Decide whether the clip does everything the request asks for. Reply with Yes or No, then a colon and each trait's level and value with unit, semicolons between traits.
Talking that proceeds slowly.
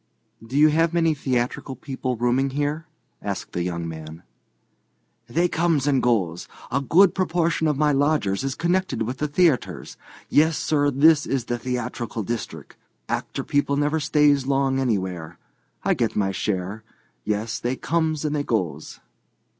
No: average, 155 wpm